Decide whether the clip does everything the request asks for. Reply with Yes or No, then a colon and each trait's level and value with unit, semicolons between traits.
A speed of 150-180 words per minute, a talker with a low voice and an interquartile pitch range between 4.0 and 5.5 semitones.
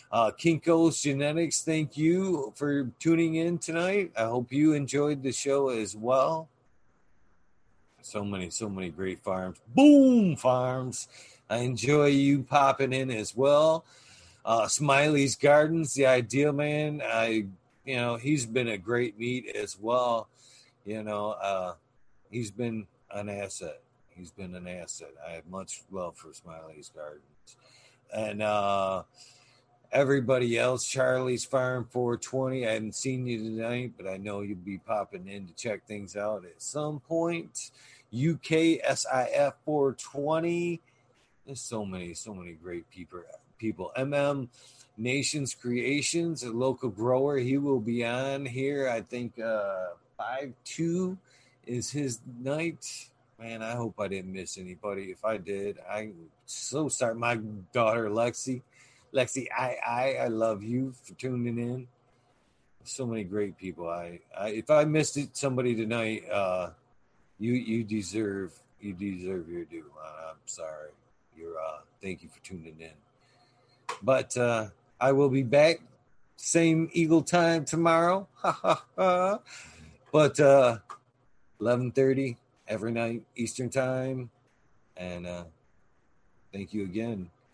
No: slow, 135 wpm; low, 120 Hz; average, 4.7 semitones